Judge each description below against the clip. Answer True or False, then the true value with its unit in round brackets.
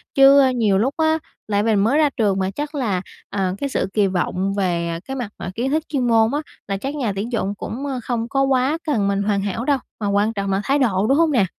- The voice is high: True (225 Hz)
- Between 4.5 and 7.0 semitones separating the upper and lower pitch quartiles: True (5.5 semitones)